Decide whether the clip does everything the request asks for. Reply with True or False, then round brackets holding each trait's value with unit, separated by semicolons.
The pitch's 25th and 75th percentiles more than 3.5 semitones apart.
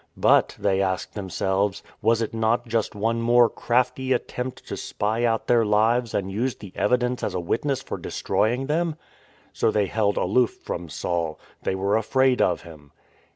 True (3.9 semitones)